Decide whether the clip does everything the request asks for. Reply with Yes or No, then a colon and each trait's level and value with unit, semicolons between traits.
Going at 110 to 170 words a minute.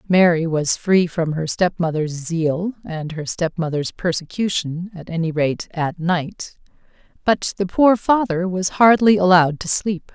Yes: average, 140 wpm